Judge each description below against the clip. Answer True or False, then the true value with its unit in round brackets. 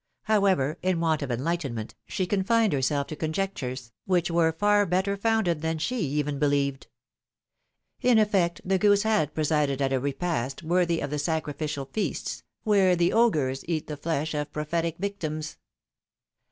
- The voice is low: False (160 Hz)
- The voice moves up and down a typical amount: True (4.7 semitones)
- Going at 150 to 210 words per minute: True (155 wpm)